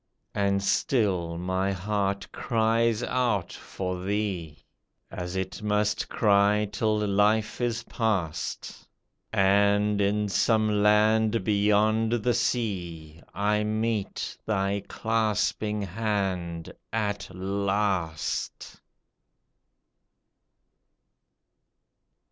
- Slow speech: Yes, slow, 80 wpm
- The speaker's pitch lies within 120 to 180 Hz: No, low, 105 Hz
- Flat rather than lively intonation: Yes, narrow, 2.0 semitones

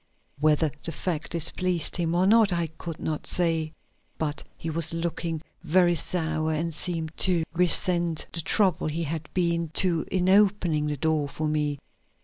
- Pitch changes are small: Yes, narrow, 2.1 semitones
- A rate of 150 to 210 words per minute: Yes, average, 160 wpm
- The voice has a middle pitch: Yes, medium, 165 Hz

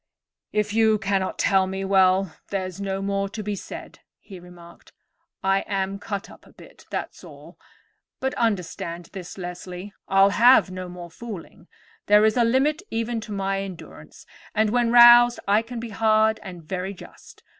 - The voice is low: No, high, 200 Hz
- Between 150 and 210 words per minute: Yes, average, 165 wpm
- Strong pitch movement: No, average, 2.8 semitones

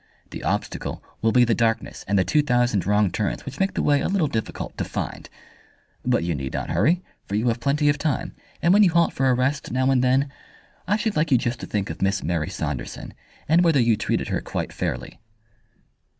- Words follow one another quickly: Yes, fast, 220 wpm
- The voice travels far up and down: Yes, wide, 6.0 semitones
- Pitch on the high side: No, low, 125 Hz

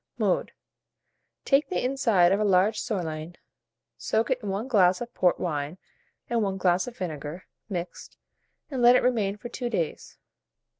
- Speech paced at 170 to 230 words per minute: No, average, 160 wpm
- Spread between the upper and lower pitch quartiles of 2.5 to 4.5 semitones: No, average, 5.2 semitones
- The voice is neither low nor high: No, high, 195 Hz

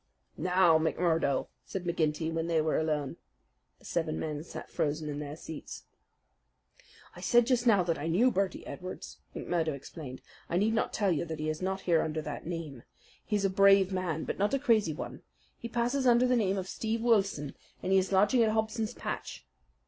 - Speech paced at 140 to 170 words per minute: No, average, 195 wpm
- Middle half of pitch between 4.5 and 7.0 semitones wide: Yes, average, 5.3 semitones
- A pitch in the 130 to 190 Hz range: Yes, medium, 185 Hz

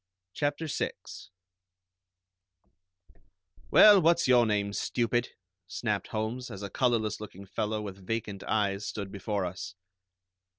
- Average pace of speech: No, slow, 115 wpm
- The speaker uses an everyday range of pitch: Yes, average, 3.4 semitones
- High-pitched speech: No, low, 105 Hz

